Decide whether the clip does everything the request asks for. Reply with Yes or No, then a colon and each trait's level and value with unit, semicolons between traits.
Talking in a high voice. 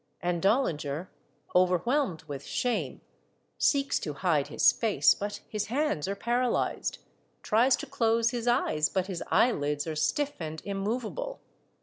Yes: high, 205 Hz